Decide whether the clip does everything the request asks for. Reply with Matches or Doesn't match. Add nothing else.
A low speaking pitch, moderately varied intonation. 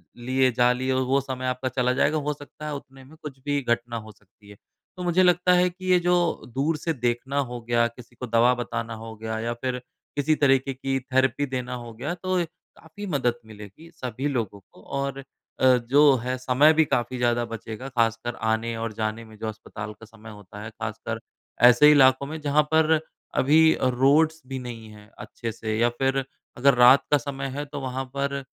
Matches